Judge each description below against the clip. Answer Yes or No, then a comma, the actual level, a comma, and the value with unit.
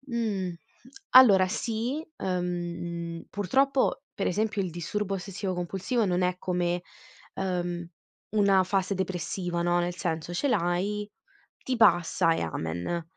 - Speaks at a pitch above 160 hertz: Yes, medium, 185 Hz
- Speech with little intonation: No, average, 3.1 semitones